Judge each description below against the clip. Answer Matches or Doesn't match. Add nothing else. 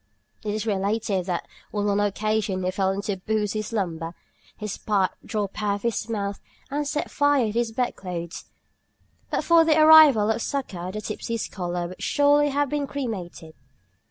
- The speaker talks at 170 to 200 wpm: Matches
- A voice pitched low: Doesn't match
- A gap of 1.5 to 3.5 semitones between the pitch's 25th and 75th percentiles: Doesn't match